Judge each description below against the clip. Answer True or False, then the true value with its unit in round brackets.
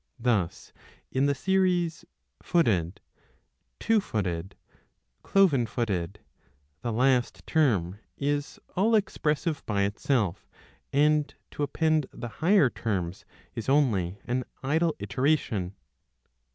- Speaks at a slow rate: True (100 wpm)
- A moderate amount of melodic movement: False (7.3 semitones)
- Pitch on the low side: True (130 Hz)